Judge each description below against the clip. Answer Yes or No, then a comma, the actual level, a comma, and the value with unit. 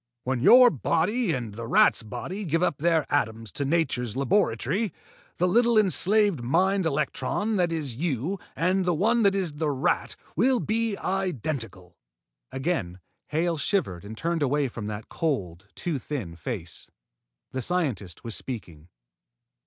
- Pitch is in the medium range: Yes, medium, 155 Hz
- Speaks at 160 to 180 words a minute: No, average, 145 wpm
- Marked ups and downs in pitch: Yes, wide, 8.2 semitones